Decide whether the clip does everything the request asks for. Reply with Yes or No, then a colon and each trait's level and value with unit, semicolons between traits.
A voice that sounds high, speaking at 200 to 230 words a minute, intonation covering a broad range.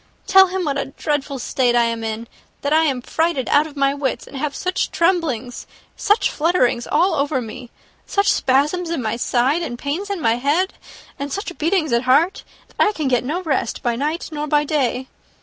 No: very high, 285 Hz; fast, 205 wpm; average, 4.8 semitones